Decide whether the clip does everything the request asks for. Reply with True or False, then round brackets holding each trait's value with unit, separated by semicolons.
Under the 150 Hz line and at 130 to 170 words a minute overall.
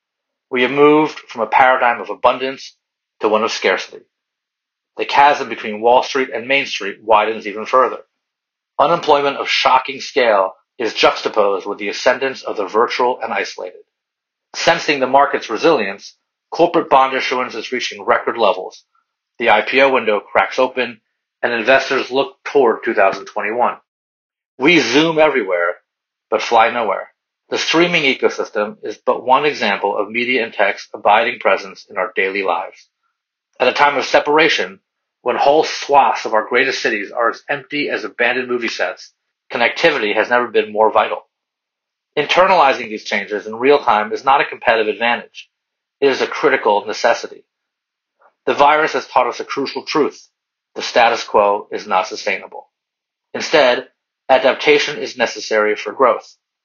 True (140 Hz; 150 wpm)